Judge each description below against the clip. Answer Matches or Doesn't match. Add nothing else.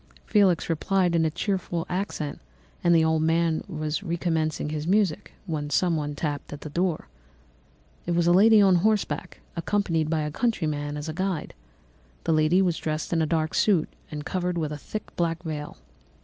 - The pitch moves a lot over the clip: Doesn't match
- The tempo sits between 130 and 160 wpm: Doesn't match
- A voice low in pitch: Doesn't match